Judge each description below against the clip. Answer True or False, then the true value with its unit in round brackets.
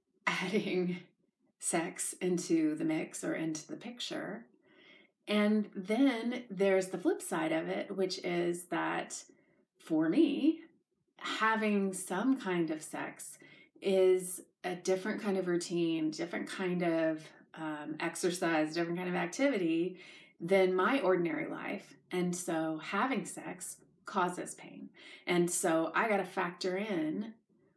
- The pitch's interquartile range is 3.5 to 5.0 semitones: True (3.9 semitones)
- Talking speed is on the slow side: True (130 wpm)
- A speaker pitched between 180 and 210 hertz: True (185 Hz)